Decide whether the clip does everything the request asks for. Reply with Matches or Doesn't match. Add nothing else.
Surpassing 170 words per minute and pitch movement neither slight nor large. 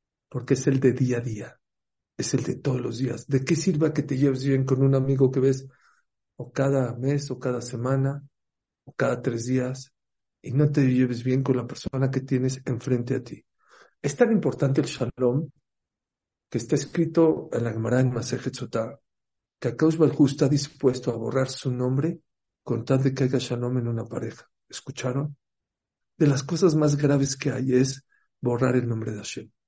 Doesn't match